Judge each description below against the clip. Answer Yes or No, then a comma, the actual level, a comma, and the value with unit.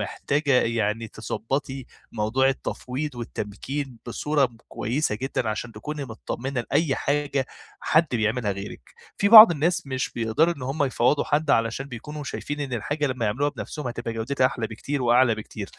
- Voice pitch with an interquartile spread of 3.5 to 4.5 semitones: Yes, average, 4.1 semitones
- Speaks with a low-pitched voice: Yes, low, 130 Hz